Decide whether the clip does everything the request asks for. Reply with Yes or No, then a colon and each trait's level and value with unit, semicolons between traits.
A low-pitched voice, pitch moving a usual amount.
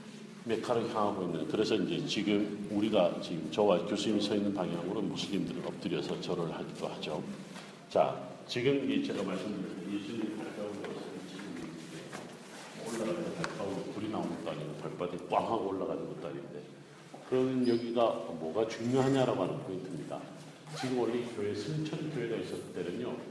Yes: low, 115 Hz; average, 4.1 semitones